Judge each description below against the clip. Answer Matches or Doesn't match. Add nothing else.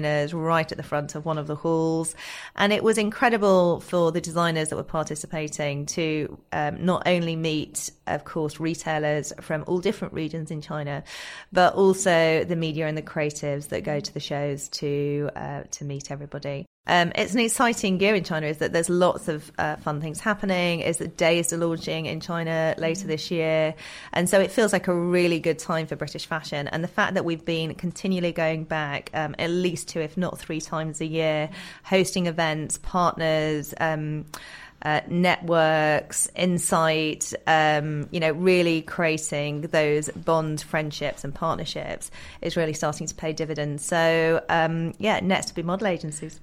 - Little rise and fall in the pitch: Matches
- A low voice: Doesn't match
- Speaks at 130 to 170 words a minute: Doesn't match